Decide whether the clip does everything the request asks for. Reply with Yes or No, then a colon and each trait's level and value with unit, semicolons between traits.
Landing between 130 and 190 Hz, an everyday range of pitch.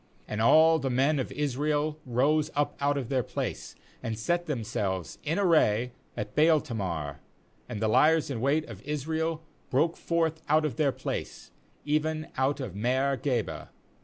Yes: medium, 140 Hz; average, 4.7 semitones